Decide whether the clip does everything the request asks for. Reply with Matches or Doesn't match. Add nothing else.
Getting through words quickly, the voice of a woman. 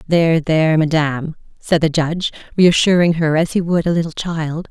Doesn't match